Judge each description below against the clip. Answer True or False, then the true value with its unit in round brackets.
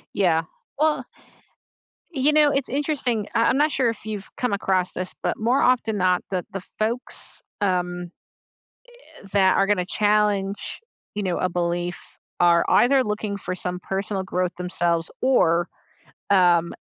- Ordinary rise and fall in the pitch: True (4.7 semitones)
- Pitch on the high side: True (200 Hz)